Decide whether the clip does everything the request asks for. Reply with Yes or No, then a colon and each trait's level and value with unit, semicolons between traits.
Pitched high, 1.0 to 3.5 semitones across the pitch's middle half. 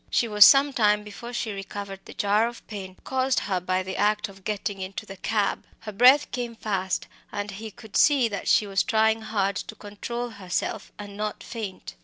Yes: high, 210 Hz; narrow, 2.4 semitones